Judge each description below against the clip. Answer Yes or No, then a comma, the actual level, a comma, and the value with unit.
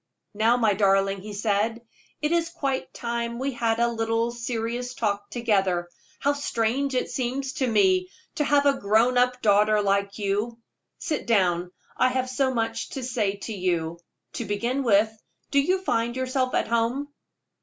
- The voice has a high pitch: Yes, high, 230 Hz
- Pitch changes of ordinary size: Yes, average, 3.9 semitones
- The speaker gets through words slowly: No, average, 165 wpm